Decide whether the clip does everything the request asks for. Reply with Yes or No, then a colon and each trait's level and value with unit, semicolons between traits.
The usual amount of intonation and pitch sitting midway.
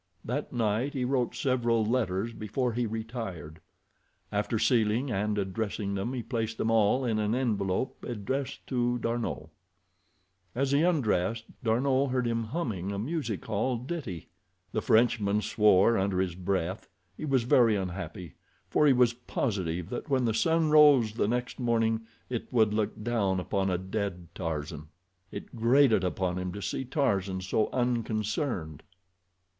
No: average, 4.0 semitones; low, 110 Hz